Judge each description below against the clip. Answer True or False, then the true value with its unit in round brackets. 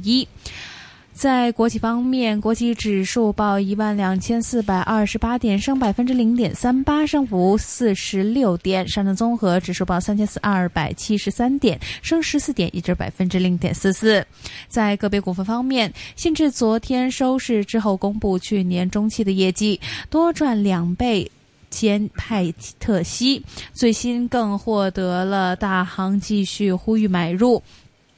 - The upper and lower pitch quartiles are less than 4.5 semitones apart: True (3.9 semitones)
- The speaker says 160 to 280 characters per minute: True (235 characters per minute)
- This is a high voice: True (210 Hz)